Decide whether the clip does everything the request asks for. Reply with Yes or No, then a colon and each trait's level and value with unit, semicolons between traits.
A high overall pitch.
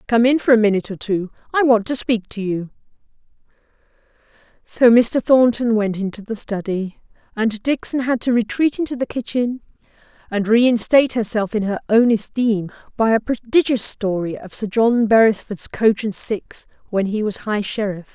Yes: high, 225 Hz